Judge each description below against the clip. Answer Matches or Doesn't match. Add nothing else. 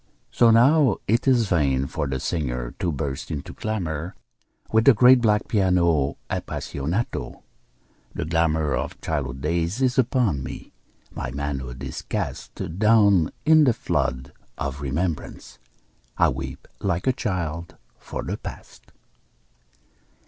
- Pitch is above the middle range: Doesn't match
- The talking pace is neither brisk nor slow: Doesn't match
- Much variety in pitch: Matches